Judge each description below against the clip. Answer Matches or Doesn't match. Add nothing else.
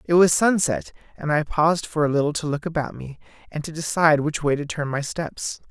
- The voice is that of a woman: Doesn't match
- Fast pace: Matches